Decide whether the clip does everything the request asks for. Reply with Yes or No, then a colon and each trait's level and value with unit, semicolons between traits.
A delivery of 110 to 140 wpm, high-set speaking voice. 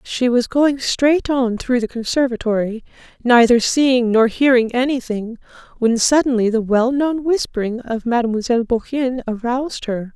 Yes: slow, 135 wpm; high, 245 Hz